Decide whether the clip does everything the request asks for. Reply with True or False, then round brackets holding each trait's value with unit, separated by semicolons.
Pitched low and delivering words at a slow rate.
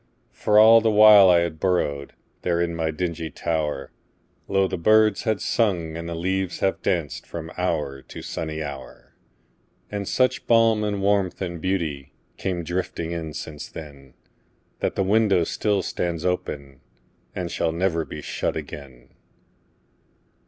True (85 Hz; 130 wpm)